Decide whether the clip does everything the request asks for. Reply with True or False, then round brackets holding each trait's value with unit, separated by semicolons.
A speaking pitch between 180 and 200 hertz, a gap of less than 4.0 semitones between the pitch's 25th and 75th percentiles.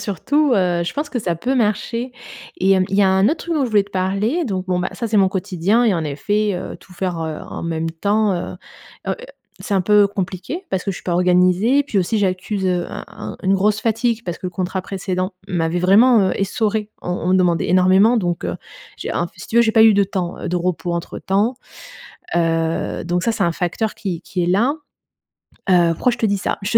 True (190 Hz; 3.4 semitones)